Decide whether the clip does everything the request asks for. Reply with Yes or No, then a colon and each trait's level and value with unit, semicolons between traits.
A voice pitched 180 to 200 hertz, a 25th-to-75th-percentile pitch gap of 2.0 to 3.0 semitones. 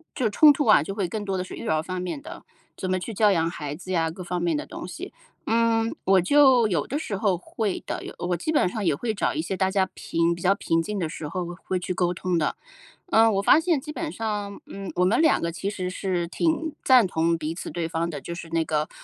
No: medium, 185 Hz; average, 4.6 semitones